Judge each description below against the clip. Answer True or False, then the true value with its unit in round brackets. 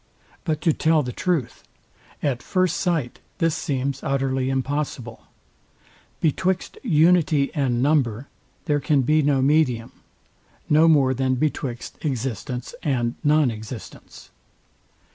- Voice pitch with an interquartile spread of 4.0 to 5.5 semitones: False (3.3 semitones)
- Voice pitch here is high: False (140 Hz)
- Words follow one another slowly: True (110 wpm)